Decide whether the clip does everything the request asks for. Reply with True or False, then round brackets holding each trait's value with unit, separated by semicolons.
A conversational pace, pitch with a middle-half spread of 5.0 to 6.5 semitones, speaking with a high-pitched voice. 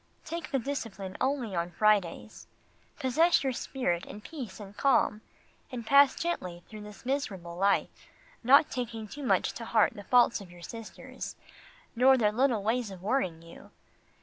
True (160 wpm; 5.3 semitones; 225 Hz)